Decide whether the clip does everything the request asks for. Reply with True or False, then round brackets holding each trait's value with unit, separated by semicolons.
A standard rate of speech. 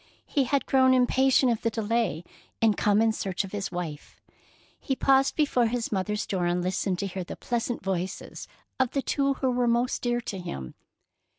True (190 wpm)